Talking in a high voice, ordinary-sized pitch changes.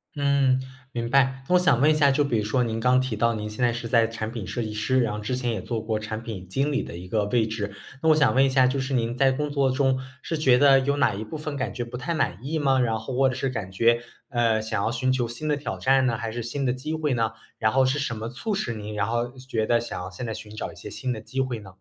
No: low, 125 Hz; average, 3.3 semitones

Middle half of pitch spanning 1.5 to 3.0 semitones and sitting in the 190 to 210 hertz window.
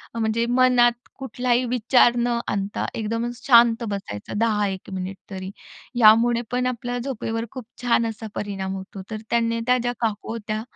No: narrow, 2.6 semitones; high, 230 Hz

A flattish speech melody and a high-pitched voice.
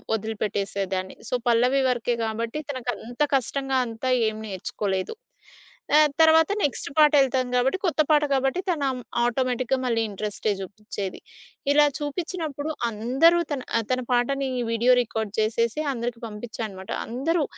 No: average, 4.0 semitones; high, 245 Hz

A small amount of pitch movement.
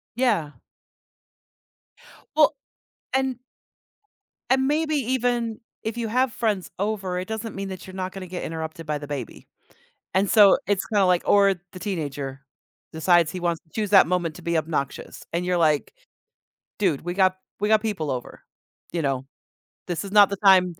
No: average, 4.7 semitones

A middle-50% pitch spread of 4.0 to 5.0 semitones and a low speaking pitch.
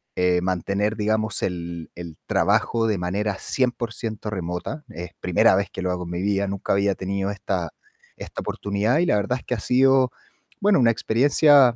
Yes: average, 4.3 semitones; low, 100 Hz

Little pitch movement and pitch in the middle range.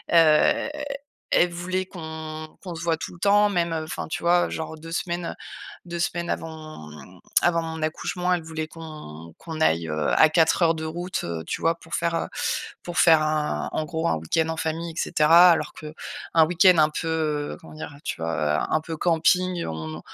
Yes: narrow, 1.8 semitones; medium, 160 Hz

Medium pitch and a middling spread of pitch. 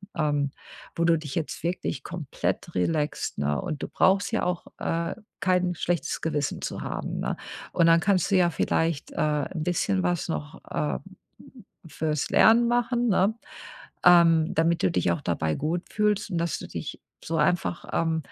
Yes: medium, 165 Hz; average, 3.2 semitones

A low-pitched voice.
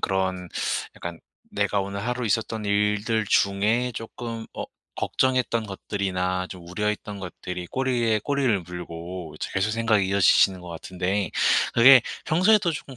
Yes: low, 100 Hz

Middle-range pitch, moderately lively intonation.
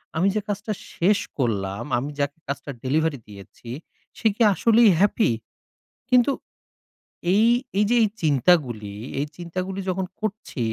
No: medium, 170 Hz; wide, 8.2 semitones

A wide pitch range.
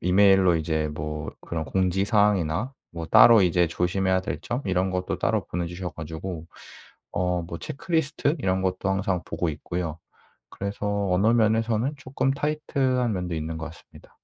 No: average, 4.5 semitones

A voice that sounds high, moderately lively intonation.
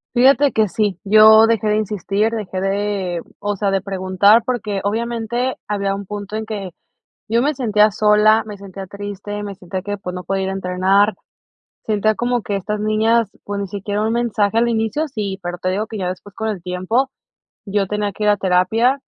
No: high, 205 Hz; narrow, 2.1 semitones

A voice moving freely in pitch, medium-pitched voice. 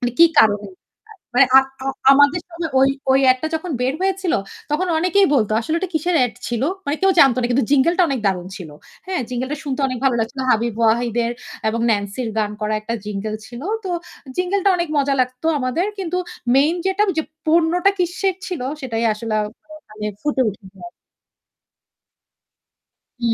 No: wide, 6.9 semitones; very high, 270 Hz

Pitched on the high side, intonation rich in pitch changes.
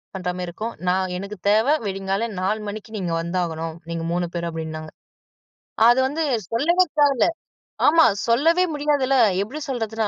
Yes: high, 210 Hz; wide, 7.0 semitones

